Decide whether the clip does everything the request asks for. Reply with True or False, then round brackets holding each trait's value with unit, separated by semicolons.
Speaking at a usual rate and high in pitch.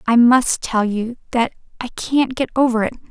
True (195 wpm; 240 Hz)